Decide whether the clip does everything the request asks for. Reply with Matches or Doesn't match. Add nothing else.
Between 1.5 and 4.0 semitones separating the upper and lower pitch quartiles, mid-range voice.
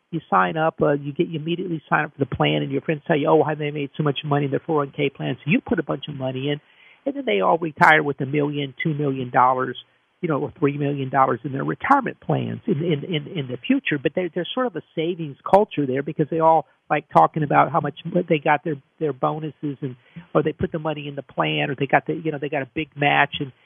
Matches